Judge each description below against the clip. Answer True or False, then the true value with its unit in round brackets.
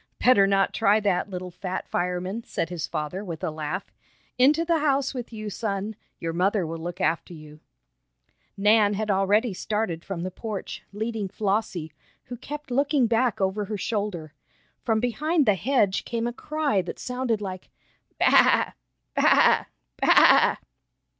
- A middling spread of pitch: True (4.4 semitones)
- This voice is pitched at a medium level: False (205 Hz)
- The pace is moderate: True (155 wpm)